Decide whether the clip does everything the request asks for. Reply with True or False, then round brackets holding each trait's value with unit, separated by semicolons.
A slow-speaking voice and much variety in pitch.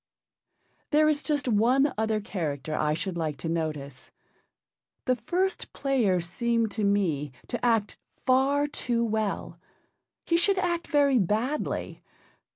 True (130 wpm; 8.0 semitones)